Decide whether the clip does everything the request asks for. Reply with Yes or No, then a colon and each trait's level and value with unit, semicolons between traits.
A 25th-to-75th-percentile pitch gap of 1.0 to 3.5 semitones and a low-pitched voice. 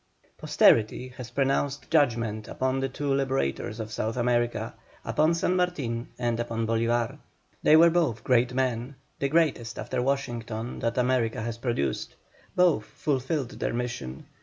Yes: average, 3.0 semitones; low, 125 Hz